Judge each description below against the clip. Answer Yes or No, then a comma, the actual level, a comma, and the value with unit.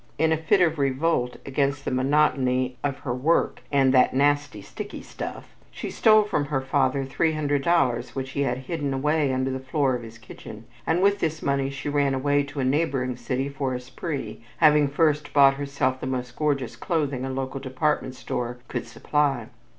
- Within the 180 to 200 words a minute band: Yes, average, 185 wpm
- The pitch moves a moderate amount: No, narrow, 2.3 semitones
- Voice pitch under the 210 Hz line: Yes, medium, 140 Hz